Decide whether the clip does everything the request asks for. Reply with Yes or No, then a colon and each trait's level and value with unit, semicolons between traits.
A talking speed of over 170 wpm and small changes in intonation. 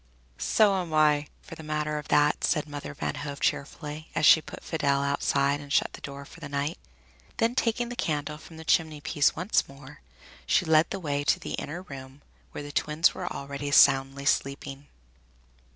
Yes: average, 190 wpm; narrow, 2.2 semitones